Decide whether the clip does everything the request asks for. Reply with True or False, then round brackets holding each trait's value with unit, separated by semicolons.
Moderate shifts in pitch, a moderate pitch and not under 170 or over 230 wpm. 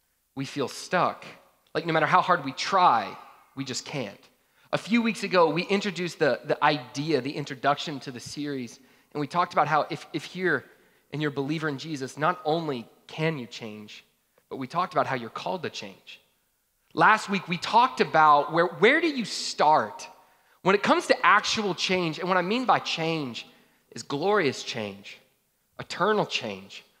True (4.8 semitones; 155 Hz; 180 wpm)